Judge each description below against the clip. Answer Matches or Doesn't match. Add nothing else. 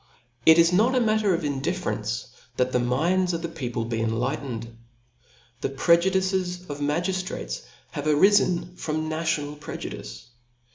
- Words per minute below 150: Matches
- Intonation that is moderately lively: Doesn't match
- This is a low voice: Doesn't match